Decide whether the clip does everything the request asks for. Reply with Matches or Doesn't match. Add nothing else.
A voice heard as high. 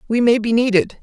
Matches